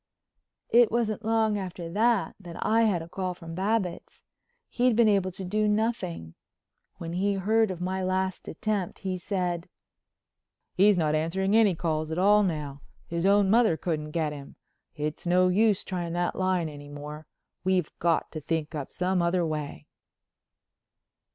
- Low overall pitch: No, medium, 185 Hz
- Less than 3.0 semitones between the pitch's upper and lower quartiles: No, average, 3.8 semitones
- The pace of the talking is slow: No, average, 160 wpm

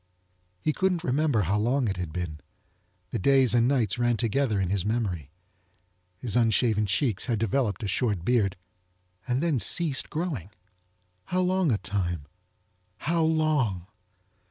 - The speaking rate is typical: Yes, average, 145 wpm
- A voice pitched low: Yes, low, 115 Hz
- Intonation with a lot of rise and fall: Yes, wide, 6.0 semitones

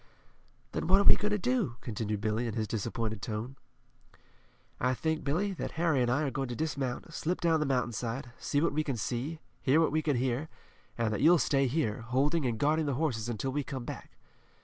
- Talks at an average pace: No, fast, 215 wpm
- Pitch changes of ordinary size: Yes, average, 4.9 semitones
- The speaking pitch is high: No, low, 135 Hz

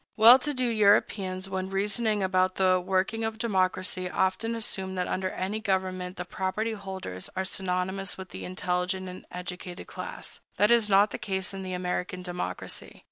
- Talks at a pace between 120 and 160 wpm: No, average, 170 wpm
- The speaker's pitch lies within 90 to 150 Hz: No, high, 190 Hz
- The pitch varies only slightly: Yes, narrow, 2.0 semitones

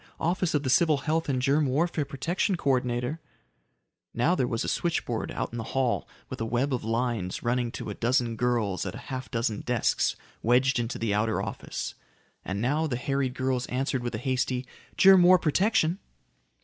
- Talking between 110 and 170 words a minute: No, average, 190 wpm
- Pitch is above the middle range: No, low, 130 Hz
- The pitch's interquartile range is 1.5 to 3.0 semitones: No, average, 3.7 semitones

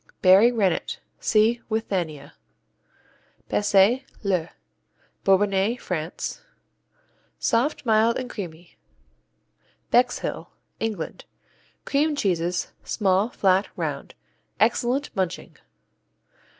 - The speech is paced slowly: Yes, slow, 75 wpm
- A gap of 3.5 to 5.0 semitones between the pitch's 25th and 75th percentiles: Yes, average, 4.4 semitones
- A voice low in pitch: No, high, 205 Hz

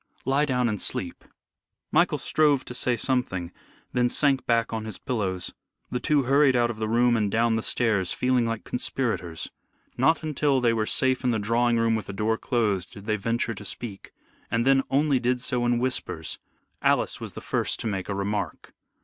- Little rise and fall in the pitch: No, average, 3.1 semitones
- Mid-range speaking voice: No, low, 120 Hz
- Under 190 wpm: No, average, 195 wpm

